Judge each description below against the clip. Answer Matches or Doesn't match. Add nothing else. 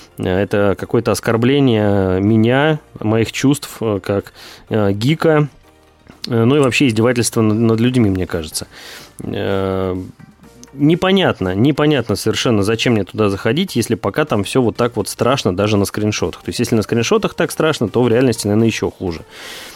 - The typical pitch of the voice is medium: Doesn't match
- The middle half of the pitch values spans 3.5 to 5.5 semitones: Matches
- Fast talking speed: Doesn't match